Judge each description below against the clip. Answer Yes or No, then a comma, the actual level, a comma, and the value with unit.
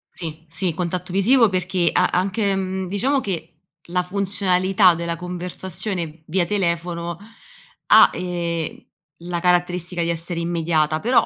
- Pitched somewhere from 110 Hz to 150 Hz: No, medium, 180 Hz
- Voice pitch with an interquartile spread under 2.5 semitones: Yes, narrow, 1.9 semitones